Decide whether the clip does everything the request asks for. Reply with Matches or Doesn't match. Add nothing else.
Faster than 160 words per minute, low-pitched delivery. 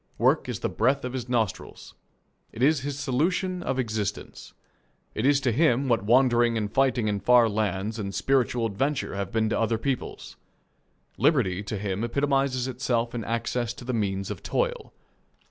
Matches